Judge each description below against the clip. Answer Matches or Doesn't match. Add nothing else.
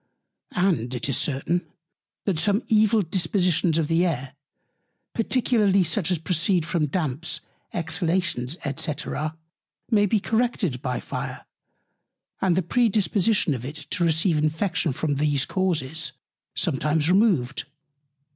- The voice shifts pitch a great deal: Doesn't match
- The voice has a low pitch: Doesn't match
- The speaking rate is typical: Doesn't match